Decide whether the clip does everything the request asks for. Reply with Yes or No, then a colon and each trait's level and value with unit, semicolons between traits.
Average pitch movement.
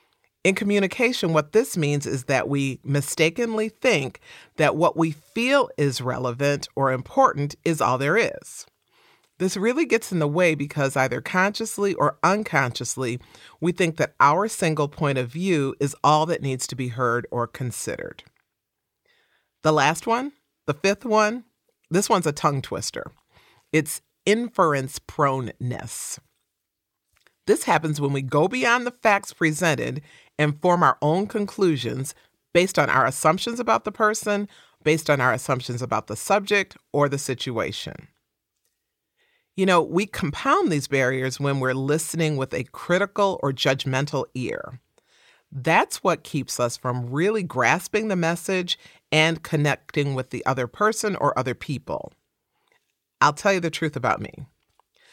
No: wide, 6.4 semitones